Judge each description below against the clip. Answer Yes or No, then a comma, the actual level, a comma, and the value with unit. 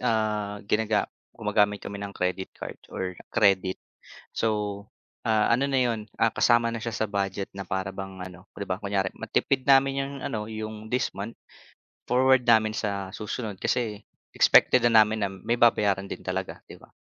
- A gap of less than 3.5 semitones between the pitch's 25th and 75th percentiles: Yes, average, 2.7 semitones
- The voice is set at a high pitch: No, low, 105 Hz